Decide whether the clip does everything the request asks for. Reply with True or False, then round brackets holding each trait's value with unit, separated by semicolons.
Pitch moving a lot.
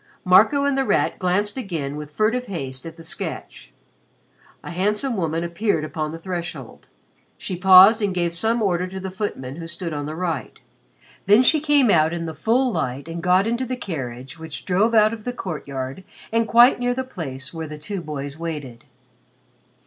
True (5.8 semitones)